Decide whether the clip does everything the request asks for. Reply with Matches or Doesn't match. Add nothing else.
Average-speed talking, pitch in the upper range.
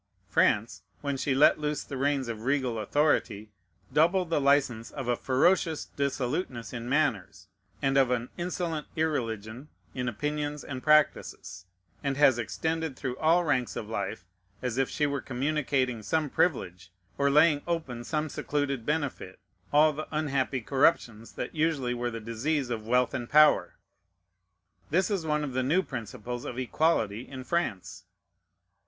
Doesn't match